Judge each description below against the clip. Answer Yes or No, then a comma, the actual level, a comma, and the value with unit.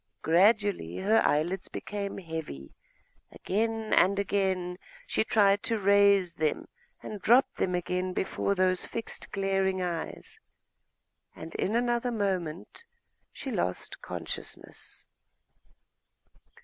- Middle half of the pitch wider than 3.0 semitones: No, narrow, 2.6 semitones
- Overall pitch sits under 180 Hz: No, high, 195 Hz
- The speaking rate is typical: No, slow, 105 wpm